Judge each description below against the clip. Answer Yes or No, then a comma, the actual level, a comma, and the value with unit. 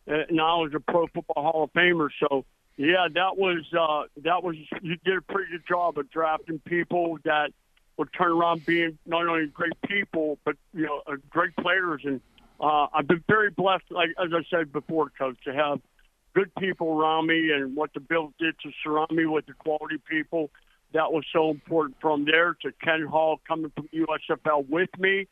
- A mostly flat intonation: Yes, narrow, 2.0 semitones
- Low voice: No, medium, 160 Hz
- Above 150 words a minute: Yes, fast, 205 wpm